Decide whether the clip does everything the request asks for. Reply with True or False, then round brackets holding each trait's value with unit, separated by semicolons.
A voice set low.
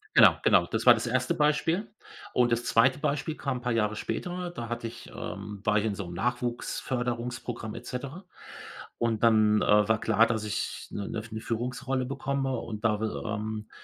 True (115 Hz)